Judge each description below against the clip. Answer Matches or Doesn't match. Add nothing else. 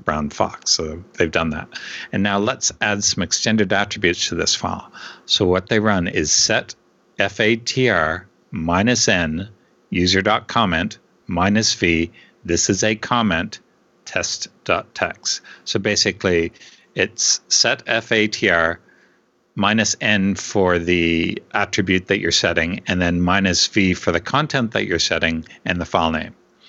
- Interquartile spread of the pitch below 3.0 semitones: Doesn't match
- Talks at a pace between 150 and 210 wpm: Doesn't match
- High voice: Doesn't match